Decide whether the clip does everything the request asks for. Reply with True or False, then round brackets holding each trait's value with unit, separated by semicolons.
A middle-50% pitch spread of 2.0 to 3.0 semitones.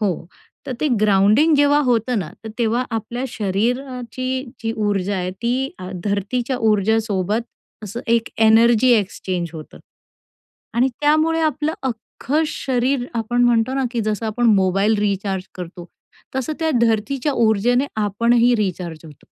False (4.0 semitones)